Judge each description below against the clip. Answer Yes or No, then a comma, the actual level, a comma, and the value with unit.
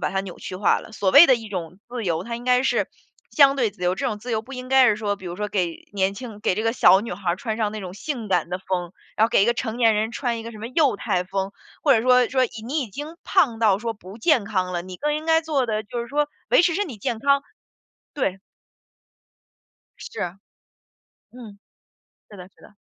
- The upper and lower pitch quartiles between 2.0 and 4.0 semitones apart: No, average, 4.7 semitones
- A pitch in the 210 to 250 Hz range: Yes, high, 220 Hz